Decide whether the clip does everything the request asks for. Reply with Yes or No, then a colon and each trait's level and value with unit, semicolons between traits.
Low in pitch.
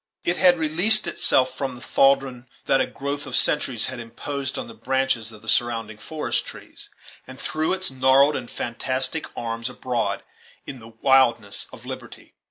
Yes: low, 130 Hz